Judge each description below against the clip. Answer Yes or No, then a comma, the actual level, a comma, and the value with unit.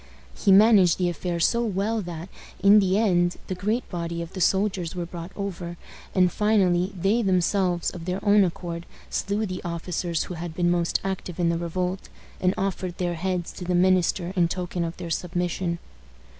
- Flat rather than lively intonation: Yes, narrow, 1.9 semitones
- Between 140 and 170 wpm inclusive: No, average, 185 wpm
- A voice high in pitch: No, medium, 180 Hz